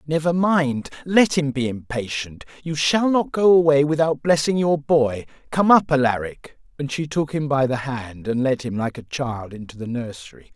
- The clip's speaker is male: Yes, male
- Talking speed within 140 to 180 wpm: No, average, 195 wpm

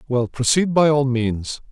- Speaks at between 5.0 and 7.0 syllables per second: No, 4.1 syllables/s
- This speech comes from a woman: No, male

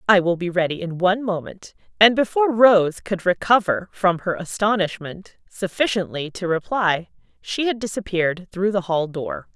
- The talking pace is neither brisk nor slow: Yes, average, 155 wpm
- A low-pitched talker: No, high, 190 Hz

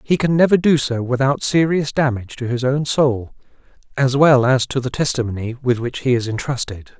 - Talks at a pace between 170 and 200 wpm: Yes, average, 195 wpm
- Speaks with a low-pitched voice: Yes, low, 130 Hz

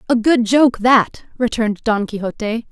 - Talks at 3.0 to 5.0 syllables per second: Yes, 4.6 syllables/s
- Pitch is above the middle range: Yes, high, 230 Hz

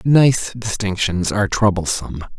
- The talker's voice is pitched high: No, low, 105 Hz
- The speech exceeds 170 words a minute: No, slow, 100 wpm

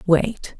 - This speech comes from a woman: Yes, female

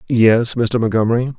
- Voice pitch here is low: Yes, low, 115 Hz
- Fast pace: No, slow, 130 wpm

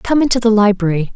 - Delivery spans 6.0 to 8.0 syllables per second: Yes, 6.4 syllables/s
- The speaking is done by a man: No, female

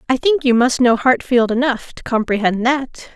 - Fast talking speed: No, average, 190 wpm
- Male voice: No, female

